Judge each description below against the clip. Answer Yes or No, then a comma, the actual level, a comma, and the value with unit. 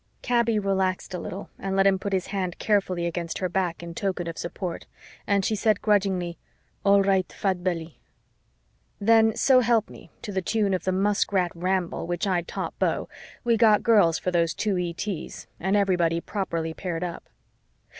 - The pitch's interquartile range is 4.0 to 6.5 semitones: No, average, 2.7 semitones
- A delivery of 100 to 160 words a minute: No, average, 175 wpm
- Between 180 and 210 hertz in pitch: Yes, high, 190 Hz